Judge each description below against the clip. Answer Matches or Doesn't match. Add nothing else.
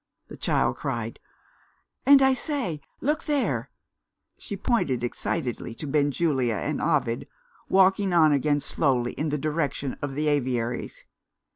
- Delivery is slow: Matches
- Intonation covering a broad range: Matches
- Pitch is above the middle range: Doesn't match